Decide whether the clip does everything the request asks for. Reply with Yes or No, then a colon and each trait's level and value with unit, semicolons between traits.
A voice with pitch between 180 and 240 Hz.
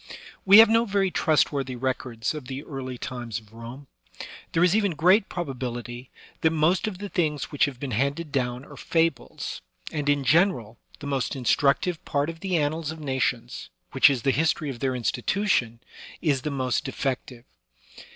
No: medium, 140 Hz